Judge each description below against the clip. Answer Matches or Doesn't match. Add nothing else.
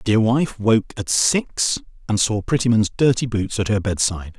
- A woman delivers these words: Doesn't match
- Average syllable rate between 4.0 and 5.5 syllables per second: Matches